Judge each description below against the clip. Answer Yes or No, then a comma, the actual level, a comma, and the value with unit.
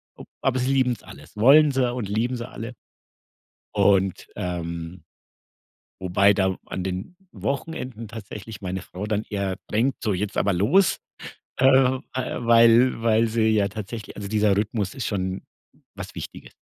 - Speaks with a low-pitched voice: Yes, low, 110 Hz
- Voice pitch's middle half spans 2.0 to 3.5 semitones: No, average, 3.9 semitones